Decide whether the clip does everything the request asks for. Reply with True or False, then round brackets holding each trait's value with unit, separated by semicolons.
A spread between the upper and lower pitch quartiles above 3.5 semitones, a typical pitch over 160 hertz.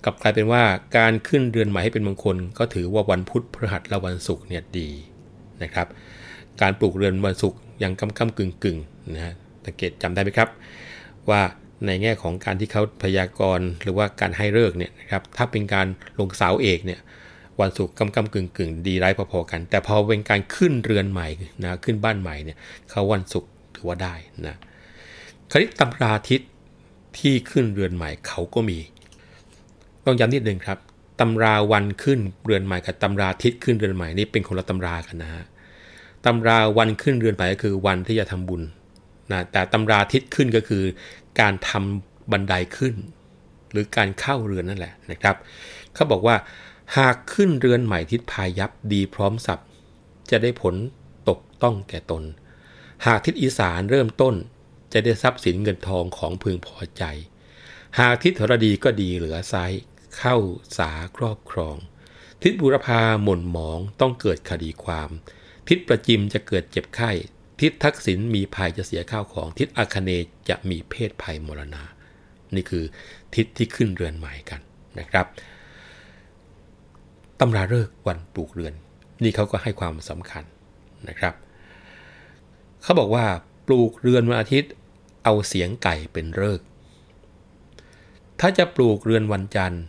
False (3.9 semitones; 95 Hz)